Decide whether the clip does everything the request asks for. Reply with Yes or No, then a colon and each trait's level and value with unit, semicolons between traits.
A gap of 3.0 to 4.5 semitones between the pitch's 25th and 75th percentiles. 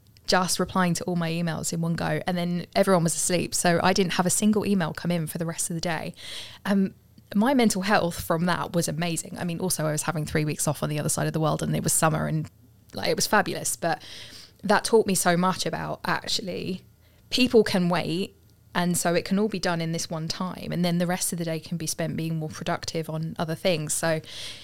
No: narrow, 2.6 semitones